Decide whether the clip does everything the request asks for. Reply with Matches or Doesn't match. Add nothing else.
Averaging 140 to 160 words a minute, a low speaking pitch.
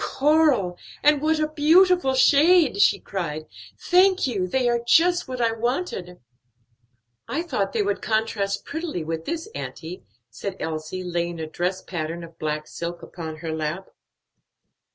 Doesn't match